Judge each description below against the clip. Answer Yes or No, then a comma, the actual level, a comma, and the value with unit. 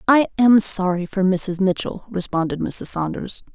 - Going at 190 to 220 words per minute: No, average, 150 wpm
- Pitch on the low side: No, high, 195 Hz